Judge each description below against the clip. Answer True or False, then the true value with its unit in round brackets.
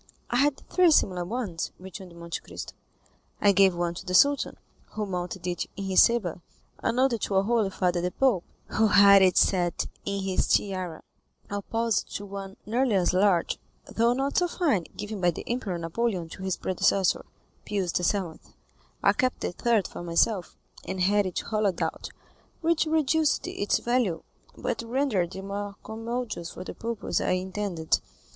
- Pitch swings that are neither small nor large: True (4.4 semitones)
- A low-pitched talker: False (200 Hz)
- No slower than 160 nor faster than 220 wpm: True (170 wpm)